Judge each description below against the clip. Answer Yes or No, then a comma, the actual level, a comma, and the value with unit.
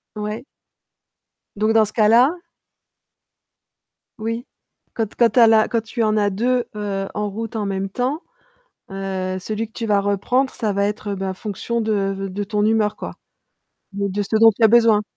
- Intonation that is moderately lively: No, narrow, 2.1 semitones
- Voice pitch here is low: No, high, 215 Hz